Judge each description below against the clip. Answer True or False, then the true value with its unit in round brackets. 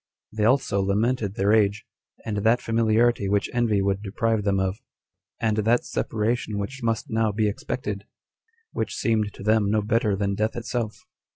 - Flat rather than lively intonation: True (2.0 semitones)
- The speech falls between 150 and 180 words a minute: True (165 wpm)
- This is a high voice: False (110 Hz)